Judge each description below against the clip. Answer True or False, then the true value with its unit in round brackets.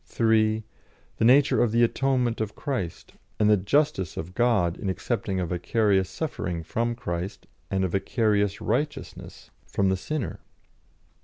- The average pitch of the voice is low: True (105 Hz)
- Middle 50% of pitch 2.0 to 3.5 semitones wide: False (4.0 semitones)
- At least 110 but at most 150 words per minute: True (145 wpm)